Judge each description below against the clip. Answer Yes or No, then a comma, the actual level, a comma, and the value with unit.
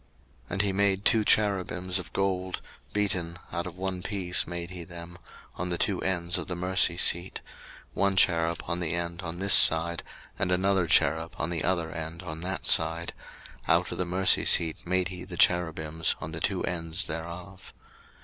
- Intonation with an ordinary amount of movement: No, narrow, 1.9 semitones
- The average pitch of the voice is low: Yes, very low, 90 Hz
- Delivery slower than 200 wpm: Yes, average, 190 wpm